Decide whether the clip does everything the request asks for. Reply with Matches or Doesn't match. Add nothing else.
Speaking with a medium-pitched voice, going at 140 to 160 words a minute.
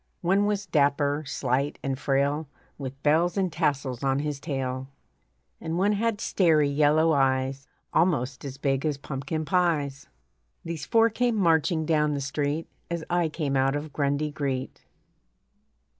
Matches